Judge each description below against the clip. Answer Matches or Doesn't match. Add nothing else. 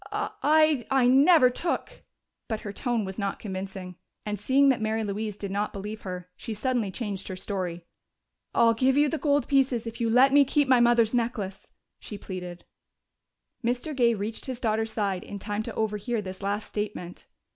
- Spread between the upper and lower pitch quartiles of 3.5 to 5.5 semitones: Matches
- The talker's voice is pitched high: Matches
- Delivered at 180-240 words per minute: Matches